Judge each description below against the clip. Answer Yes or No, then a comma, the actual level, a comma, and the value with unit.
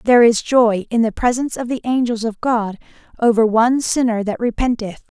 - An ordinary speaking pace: Yes, average, 185 wpm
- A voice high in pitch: Yes, high, 230 Hz